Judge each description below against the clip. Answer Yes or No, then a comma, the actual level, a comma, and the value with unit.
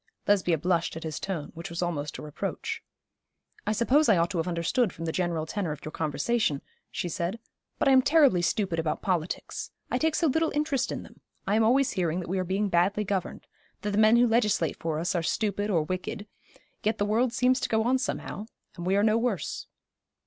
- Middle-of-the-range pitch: No, high, 195 Hz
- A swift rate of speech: Yes, fast, 220 wpm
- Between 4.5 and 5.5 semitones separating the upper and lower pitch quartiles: Yes, average, 5.1 semitones